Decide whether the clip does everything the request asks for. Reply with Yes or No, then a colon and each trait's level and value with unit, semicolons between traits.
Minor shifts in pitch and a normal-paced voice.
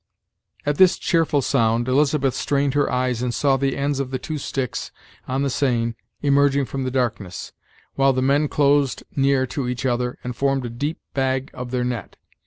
Yes: narrow, 2.1 semitones; average, 190 wpm